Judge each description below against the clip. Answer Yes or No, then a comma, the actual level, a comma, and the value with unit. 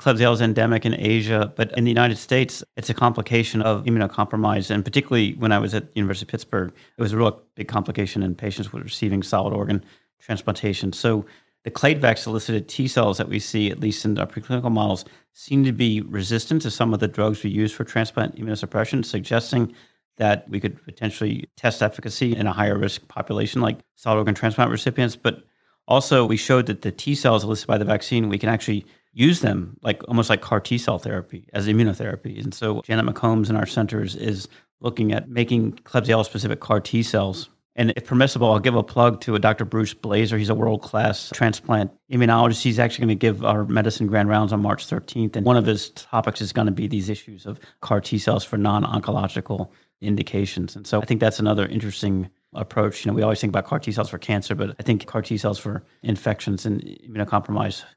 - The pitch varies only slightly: Yes, narrow, 2.1 semitones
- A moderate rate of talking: No, fast, 210 wpm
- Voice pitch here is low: Yes, low, 110 Hz